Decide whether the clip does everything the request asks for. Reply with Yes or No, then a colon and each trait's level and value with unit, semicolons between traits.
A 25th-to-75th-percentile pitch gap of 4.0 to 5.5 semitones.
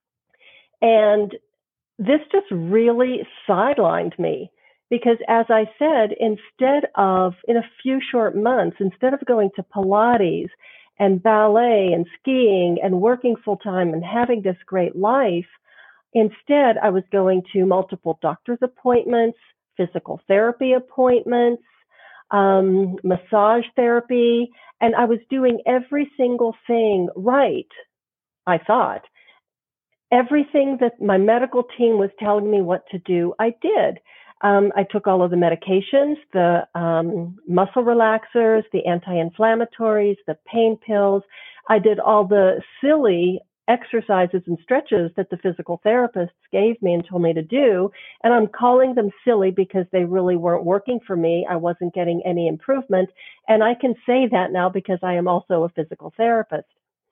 Yes: average, 4.5 semitones